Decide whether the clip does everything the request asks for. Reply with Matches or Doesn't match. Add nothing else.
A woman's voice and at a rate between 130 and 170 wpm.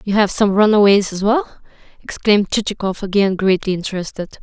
Matches